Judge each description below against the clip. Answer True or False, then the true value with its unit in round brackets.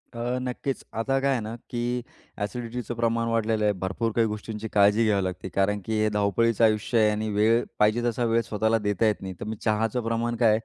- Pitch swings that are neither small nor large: False (1.9 semitones)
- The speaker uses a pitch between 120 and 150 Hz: False (110 Hz)